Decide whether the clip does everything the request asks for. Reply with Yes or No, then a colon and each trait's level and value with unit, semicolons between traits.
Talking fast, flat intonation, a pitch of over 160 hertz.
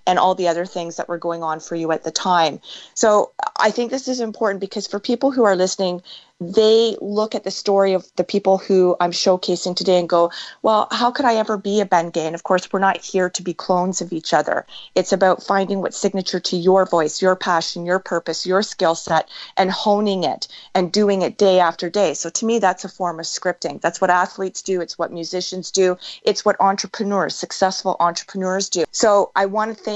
Yes: fast, 225 wpm; narrow, 2.3 semitones; medium, 185 Hz